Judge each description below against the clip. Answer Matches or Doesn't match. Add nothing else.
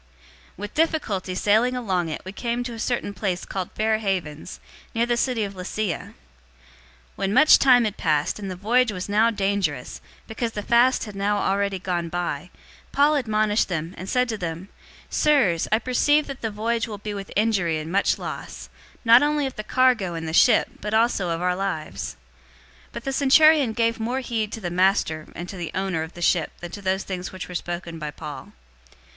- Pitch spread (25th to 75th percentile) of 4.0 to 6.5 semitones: Matches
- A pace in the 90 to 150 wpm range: Doesn't match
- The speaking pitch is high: Matches